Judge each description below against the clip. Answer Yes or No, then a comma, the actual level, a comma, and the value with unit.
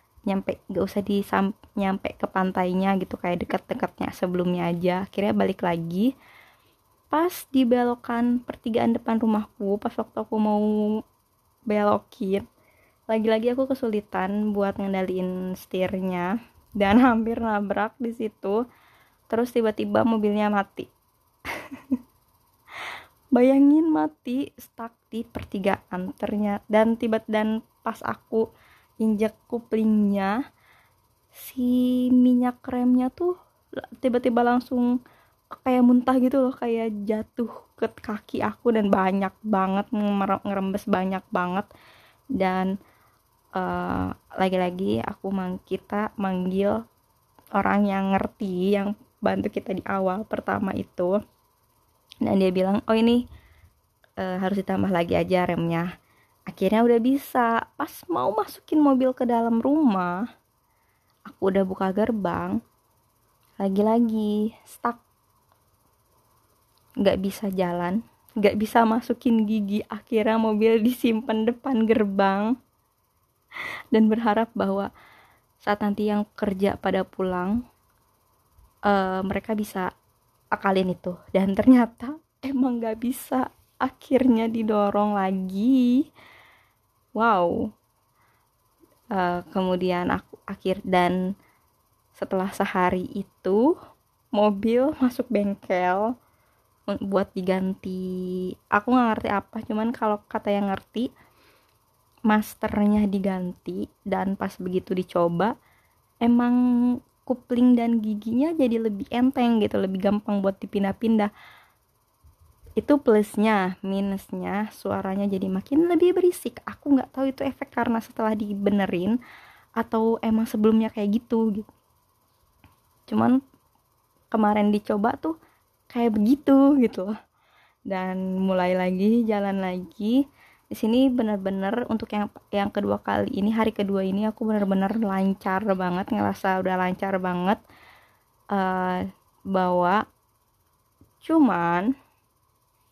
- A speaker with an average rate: Yes, average, 105 wpm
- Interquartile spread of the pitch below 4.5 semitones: Yes, average, 3.6 semitones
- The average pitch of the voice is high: Yes, high, 210 Hz